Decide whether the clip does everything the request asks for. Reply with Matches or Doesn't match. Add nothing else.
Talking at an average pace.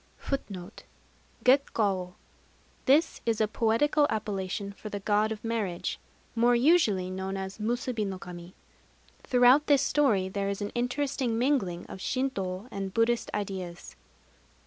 Doesn't match